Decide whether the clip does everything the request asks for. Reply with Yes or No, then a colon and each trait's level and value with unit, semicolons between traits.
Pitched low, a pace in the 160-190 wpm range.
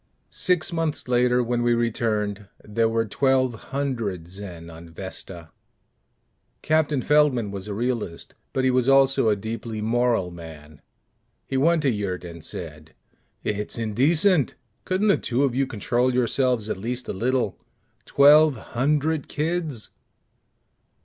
No: low, 120 Hz; slow, 135 wpm